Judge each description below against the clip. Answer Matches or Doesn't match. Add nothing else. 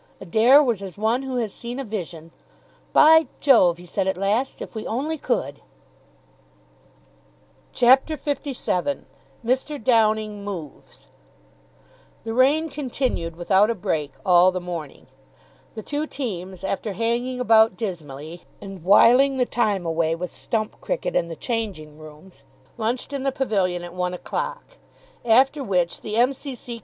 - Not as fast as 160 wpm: Matches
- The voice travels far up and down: Matches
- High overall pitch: Matches